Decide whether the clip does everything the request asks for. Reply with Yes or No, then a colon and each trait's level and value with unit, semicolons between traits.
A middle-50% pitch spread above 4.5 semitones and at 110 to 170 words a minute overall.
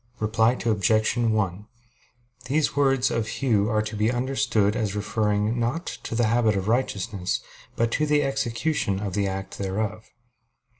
No: average, 2.8 semitones; average, 150 wpm